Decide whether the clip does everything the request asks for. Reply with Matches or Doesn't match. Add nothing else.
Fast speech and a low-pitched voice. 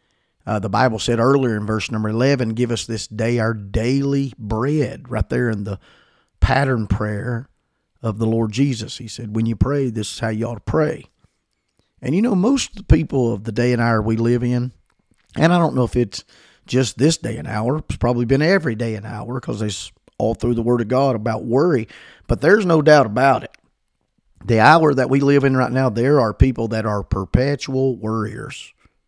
Matches